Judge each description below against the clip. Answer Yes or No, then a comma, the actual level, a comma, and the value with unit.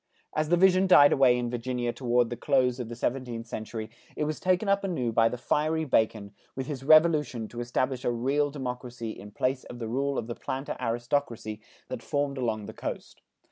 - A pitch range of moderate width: Yes, average, 3.5 semitones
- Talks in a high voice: No, low, 125 Hz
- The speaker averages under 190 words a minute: No, average, 200 wpm